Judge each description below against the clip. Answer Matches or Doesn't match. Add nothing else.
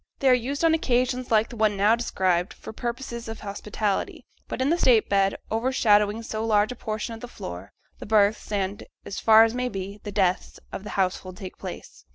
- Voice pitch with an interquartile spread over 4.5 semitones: Doesn't match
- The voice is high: Matches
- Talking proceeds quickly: Matches